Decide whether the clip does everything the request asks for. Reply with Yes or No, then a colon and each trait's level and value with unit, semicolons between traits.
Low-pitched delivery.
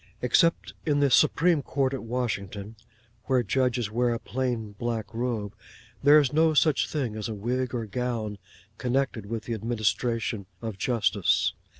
Yes: low, 120 Hz